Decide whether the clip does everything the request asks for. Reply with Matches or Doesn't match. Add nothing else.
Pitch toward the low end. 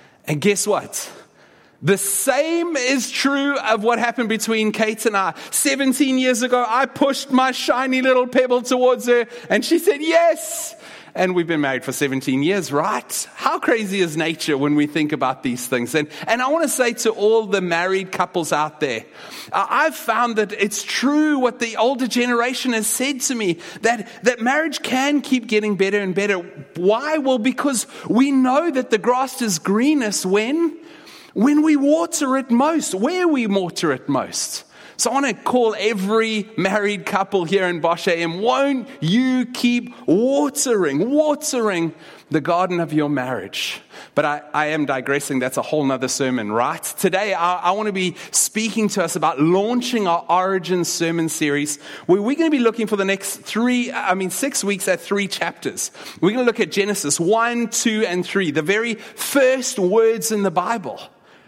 Doesn't match